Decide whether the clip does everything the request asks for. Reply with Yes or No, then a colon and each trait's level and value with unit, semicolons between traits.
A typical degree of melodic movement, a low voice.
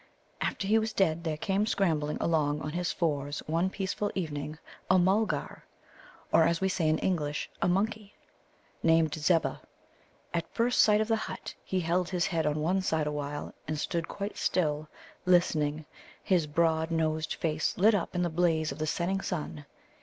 No: average, 3.4 semitones; medium, 165 Hz